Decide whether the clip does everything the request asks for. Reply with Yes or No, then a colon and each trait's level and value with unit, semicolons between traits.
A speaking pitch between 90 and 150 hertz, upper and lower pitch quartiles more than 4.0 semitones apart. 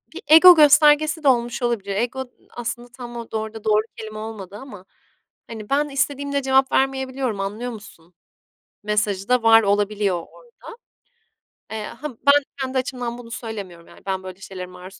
No: high, 235 Hz; average, 4.4 semitones